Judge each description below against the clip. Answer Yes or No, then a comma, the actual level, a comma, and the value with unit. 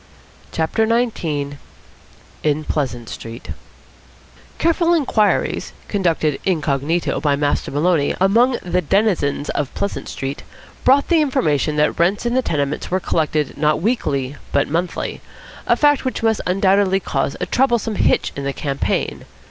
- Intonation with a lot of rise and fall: Yes, wide, 7.4 semitones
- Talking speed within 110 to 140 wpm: Yes, slow, 135 wpm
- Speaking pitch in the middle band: Yes, medium, 170 Hz